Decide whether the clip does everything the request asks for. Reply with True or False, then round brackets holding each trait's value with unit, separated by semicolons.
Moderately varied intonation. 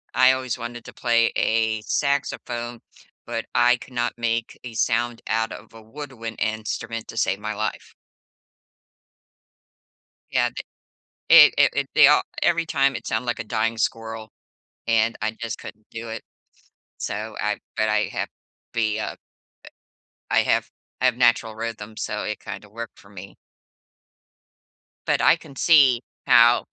False (1.7 semitones)